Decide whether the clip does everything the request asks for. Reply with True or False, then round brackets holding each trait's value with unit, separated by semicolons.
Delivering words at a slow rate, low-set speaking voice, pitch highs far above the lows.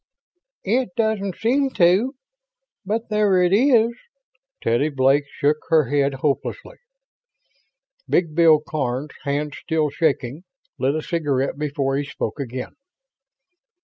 False (115 wpm; 155 Hz; 5.9 semitones)